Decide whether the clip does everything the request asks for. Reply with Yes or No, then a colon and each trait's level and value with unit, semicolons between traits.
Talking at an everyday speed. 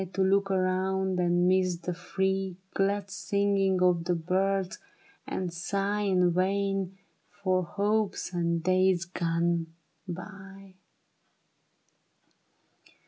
No: slow, 100 wpm